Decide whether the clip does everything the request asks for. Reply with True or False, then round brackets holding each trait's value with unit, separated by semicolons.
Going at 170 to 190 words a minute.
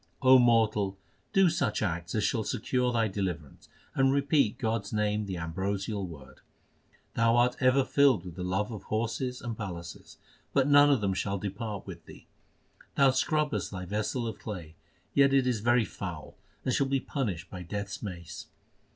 True (175 wpm)